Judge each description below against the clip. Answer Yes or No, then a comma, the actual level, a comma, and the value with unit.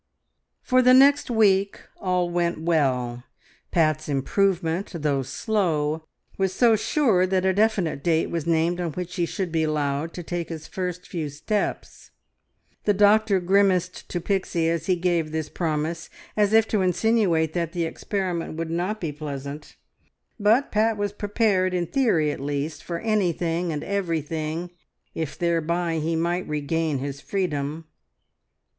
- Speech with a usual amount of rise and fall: Yes, average, 3.8 semitones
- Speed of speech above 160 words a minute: No, average, 150 wpm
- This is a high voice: No, medium, 170 Hz